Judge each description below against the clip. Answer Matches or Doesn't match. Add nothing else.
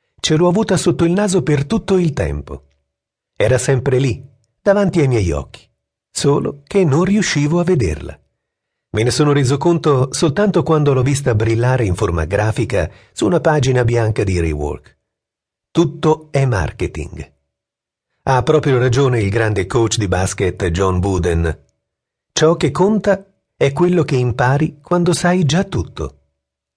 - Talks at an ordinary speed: Matches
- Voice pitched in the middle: Doesn't match